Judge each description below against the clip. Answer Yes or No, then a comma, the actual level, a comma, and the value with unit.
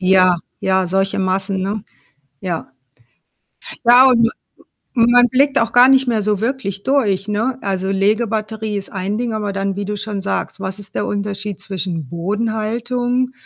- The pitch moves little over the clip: No, average, 3.3 semitones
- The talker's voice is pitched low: No, high, 210 Hz